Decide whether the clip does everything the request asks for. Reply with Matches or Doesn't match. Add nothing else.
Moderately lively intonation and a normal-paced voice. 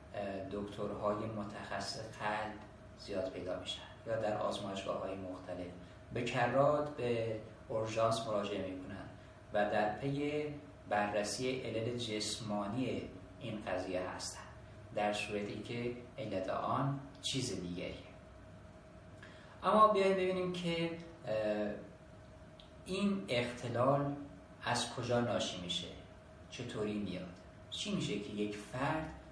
Doesn't match